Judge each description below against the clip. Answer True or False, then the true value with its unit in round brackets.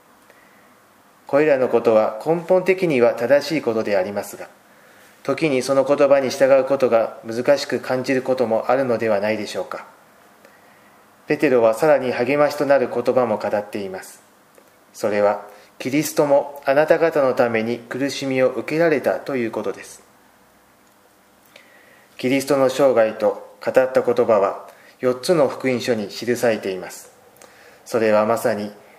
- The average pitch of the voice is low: True (130 Hz)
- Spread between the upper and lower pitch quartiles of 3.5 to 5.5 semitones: True (5.1 semitones)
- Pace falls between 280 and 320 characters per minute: True (295 characters per minute)